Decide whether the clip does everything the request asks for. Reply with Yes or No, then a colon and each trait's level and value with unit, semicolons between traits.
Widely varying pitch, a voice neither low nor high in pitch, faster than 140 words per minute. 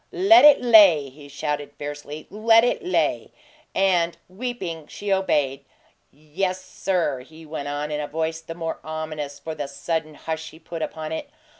No: average, 4.0 semitones; medium, 160 Hz; average, 165 wpm